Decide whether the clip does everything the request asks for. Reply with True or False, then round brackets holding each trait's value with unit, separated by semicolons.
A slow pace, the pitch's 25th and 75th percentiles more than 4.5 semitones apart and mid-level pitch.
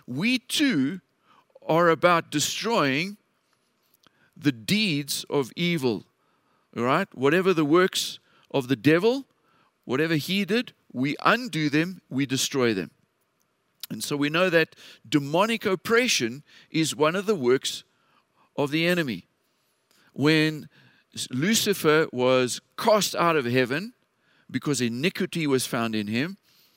True (120 wpm; 5.5 semitones; 160 Hz)